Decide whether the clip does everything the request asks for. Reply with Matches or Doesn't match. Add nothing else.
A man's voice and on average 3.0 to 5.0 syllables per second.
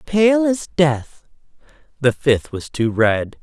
Matches